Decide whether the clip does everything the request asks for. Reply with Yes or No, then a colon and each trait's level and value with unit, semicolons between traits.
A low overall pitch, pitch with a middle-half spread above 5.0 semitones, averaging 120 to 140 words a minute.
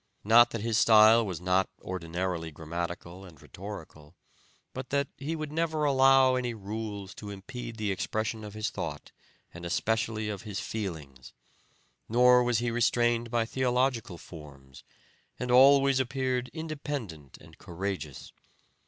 Yes: low, 110 Hz; wide, 5.5 semitones; slow, 135 wpm